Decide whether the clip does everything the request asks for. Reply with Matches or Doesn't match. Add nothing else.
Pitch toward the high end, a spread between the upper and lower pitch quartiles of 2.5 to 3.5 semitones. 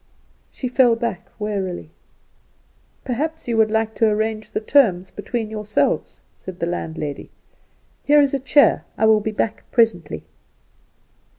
Matches